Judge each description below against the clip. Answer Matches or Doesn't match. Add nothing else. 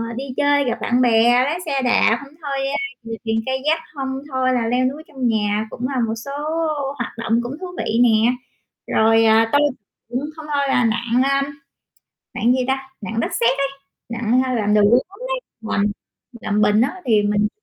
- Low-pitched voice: Doesn't match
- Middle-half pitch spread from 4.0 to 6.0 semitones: Doesn't match